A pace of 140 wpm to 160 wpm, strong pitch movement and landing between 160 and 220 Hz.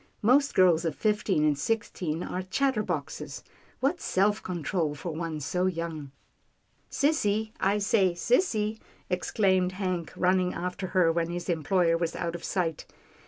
No: average, 155 wpm; average, 3.8 semitones; medium, 185 Hz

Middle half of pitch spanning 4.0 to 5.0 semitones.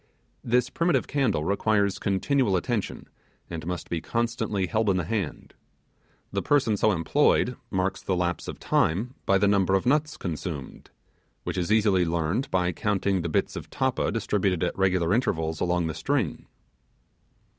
Yes: average, 4.7 semitones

